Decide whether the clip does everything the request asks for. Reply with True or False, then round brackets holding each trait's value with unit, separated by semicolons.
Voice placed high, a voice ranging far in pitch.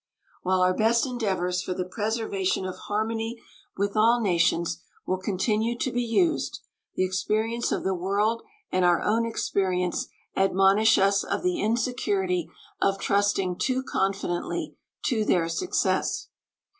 False (200 Hz; 3.5 semitones)